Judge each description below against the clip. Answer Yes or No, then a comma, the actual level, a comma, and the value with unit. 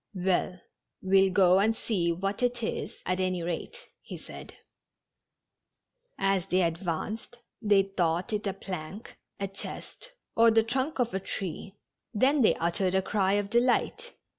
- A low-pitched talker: No, high, 195 Hz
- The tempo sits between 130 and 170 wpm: Yes, average, 150 wpm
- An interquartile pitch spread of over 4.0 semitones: No, average, 3.5 semitones